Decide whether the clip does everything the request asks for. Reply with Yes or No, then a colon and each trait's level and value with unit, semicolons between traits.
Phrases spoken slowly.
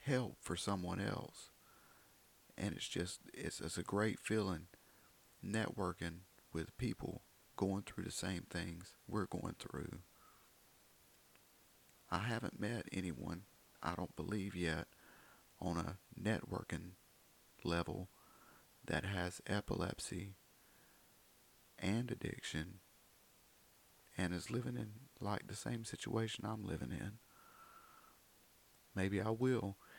Yes: slow, 110 wpm